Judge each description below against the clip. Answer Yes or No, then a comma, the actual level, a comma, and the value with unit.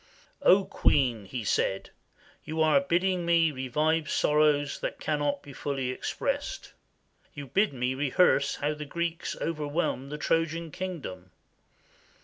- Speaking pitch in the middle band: Yes, medium, 150 Hz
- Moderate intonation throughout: Yes, average, 3.2 semitones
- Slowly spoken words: Yes, slow, 130 wpm